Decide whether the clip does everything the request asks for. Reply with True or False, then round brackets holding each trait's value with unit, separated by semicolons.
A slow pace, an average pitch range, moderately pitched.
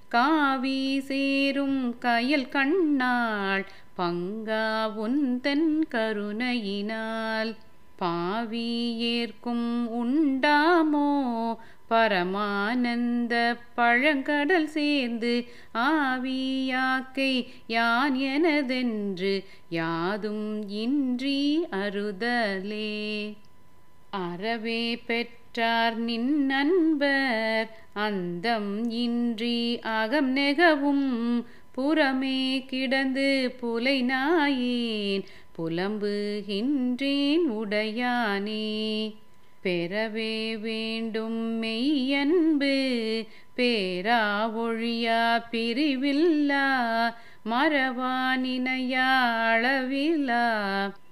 False (45 wpm; 3.5 semitones; 235 Hz)